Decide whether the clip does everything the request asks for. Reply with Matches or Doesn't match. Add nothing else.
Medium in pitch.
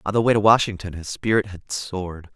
Doesn't match